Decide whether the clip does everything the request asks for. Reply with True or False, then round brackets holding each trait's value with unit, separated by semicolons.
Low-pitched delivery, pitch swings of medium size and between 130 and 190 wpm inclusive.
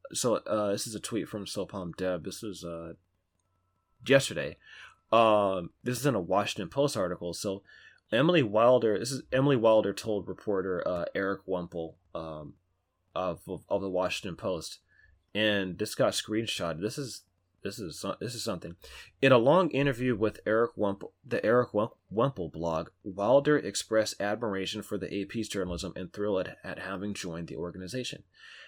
True (100 Hz; 3.4 semitones; 160 wpm)